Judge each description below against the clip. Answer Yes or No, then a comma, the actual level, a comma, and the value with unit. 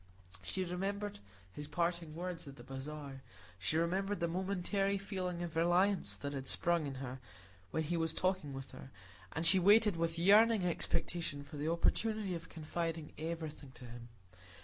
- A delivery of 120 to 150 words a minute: No, average, 165 wpm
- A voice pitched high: No, medium, 170 Hz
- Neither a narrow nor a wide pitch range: Yes, average, 3.9 semitones